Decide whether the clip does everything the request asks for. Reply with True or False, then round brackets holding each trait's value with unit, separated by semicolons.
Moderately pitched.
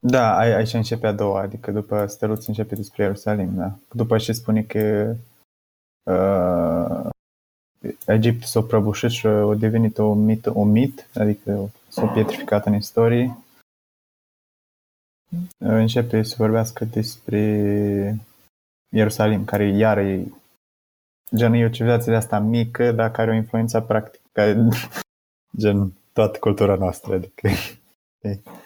False (105 Hz)